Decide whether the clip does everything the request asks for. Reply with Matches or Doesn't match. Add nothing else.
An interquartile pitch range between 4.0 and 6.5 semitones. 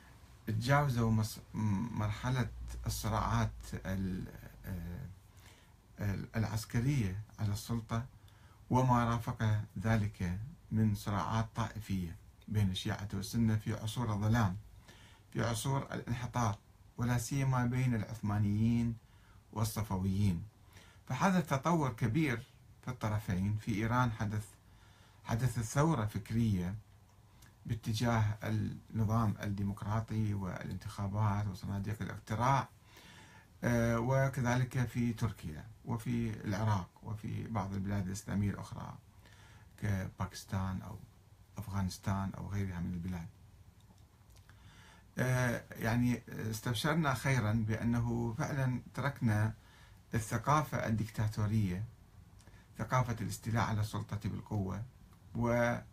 Doesn't match